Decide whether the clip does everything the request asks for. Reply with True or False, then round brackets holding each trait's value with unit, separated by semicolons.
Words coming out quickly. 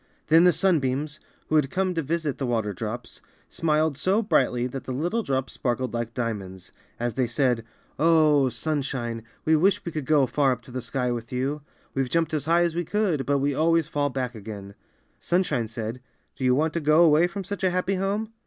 True (210 wpm)